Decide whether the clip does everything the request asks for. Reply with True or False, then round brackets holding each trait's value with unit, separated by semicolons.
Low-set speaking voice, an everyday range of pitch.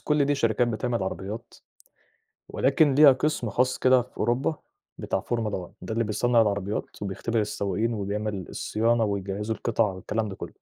True (110 Hz; 3.1 semitones)